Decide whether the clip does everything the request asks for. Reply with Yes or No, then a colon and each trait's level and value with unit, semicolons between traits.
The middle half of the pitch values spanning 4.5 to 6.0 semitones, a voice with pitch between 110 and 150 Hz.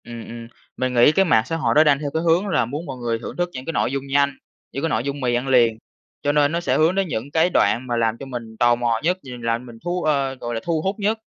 Yes: average, 5.1 semitones; low, 135 Hz